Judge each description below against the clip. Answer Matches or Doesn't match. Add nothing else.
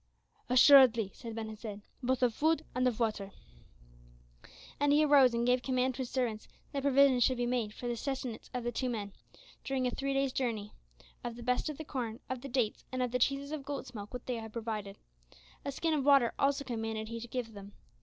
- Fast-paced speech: Matches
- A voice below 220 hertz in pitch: Doesn't match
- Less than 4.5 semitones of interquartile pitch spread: Matches